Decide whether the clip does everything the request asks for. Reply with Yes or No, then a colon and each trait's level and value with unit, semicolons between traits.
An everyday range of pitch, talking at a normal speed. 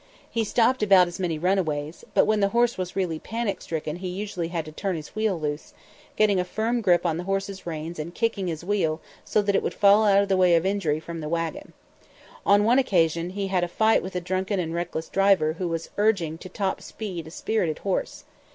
No: average, 3.4 semitones; fast, 230 wpm